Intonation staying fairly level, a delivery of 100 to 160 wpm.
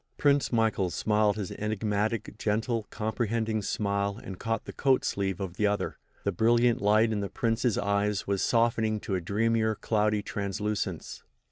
Yes: narrow, 2.0 semitones; average, 155 wpm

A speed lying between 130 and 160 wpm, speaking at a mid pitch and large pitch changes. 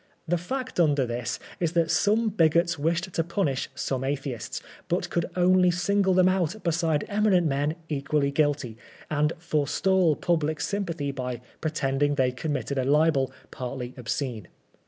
No: average, 150 wpm; medium, 155 Hz; average, 4.3 semitones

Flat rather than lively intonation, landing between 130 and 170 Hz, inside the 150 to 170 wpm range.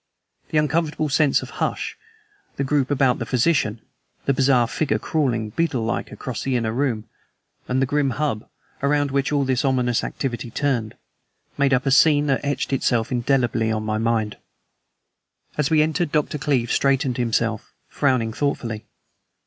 No: average, 3.7 semitones; low, 135 Hz; average, 155 wpm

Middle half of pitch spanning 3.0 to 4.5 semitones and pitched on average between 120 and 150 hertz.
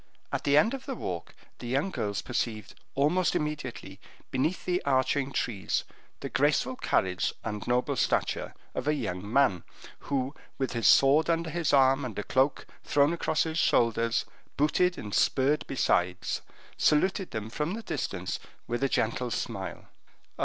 No: average, 4.9 semitones; low, 135 Hz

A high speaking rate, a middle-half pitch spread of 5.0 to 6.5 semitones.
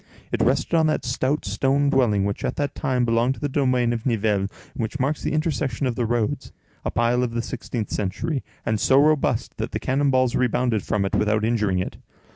No: fast, 210 wpm; average, 3.7 semitones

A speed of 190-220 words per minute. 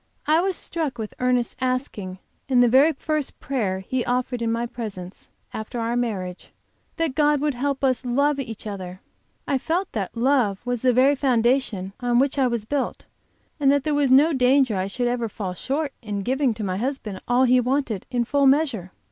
Yes: average, 200 wpm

